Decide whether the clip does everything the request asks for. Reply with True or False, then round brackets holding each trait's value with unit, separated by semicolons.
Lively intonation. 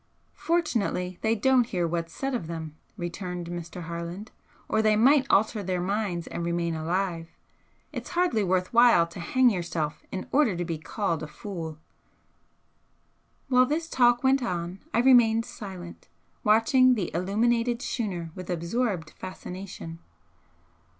True (5.7 semitones)